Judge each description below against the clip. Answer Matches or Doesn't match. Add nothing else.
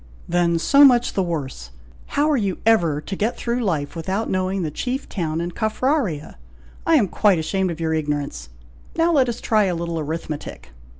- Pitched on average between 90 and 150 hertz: Doesn't match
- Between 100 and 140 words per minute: Doesn't match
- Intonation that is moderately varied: Doesn't match